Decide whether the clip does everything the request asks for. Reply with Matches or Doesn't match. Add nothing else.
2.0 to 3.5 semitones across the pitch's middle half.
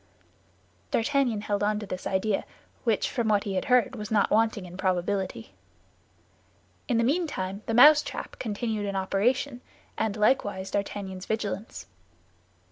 Matches